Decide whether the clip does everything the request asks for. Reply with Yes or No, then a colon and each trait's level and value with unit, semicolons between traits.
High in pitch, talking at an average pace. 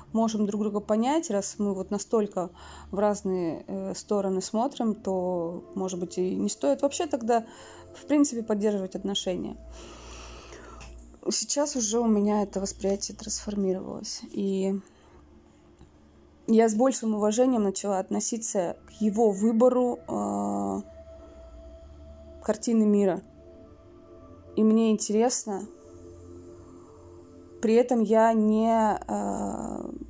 No: high, 200 Hz; slow, 105 wpm